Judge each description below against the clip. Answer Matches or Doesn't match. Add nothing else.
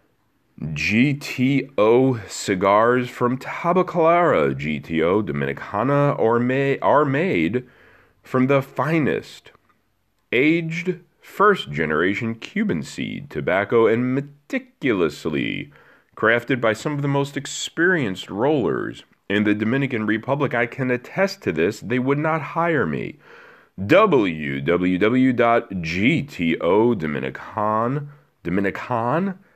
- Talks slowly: Matches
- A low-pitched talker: Matches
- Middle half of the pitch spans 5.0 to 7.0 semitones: Matches